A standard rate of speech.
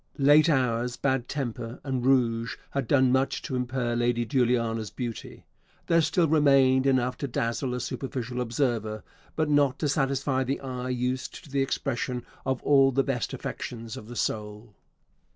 Yes: average, 160 wpm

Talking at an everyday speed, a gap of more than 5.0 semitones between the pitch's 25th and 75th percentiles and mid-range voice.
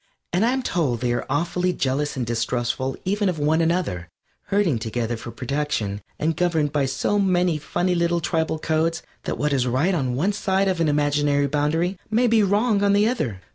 Yes: average, 190 wpm; wide, 5.6 semitones; medium, 160 Hz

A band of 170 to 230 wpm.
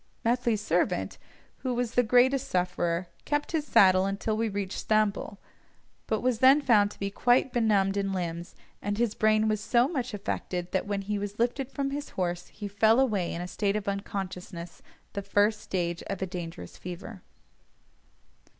Yes: average, 175 wpm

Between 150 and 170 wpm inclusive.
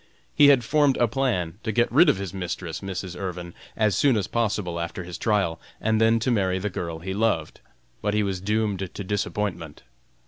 No: average, 200 wpm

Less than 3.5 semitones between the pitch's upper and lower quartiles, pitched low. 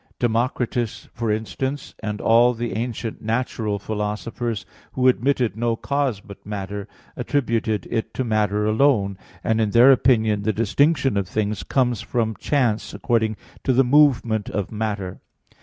Yes: average, 2.8 semitones; low, 115 Hz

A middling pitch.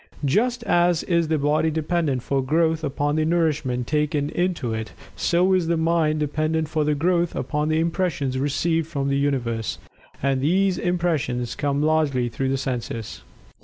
Yes: medium, 155 Hz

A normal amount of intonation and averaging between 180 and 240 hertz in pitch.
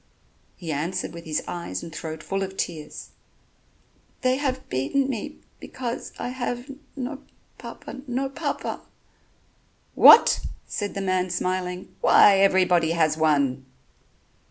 No: wide, 7.5 semitones; medium, 185 Hz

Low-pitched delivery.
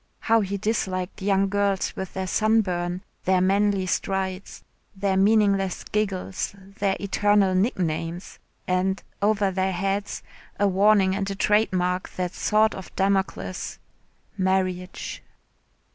No: high, 195 Hz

